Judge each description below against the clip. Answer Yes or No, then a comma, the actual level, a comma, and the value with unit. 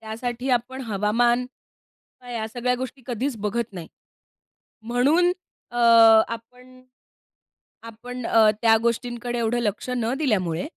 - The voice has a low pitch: No, high, 240 Hz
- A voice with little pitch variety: Yes, narrow, 1.9 semitones